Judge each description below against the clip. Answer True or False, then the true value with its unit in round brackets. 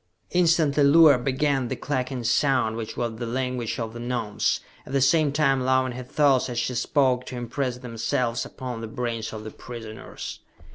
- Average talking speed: True (180 wpm)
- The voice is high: False (125 Hz)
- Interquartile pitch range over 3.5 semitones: False (2.7 semitones)